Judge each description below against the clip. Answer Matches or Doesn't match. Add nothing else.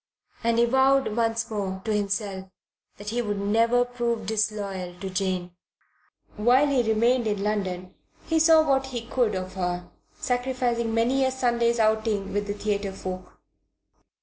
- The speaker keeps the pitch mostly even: Doesn't match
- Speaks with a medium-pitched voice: Doesn't match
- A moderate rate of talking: Matches